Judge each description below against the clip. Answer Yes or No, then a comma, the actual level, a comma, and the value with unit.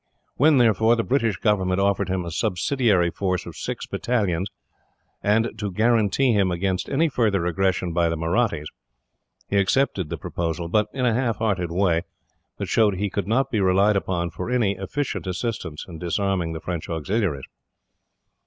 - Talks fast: No, average, 165 wpm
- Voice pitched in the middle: No, low, 100 Hz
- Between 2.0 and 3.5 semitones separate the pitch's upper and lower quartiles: No, average, 4.4 semitones